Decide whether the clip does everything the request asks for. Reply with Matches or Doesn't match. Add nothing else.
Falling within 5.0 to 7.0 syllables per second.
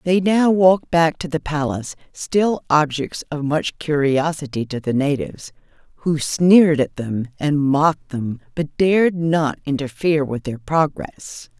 Doesn't match